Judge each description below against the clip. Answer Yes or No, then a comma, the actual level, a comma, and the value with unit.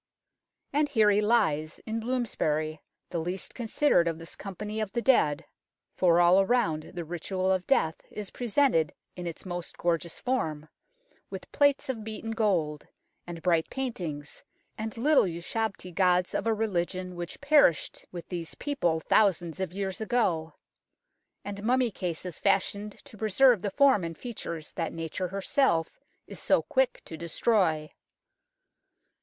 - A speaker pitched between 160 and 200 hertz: Yes, high, 190 Hz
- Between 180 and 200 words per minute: No, average, 145 wpm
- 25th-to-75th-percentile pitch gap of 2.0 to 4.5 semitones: No, average, 5.0 semitones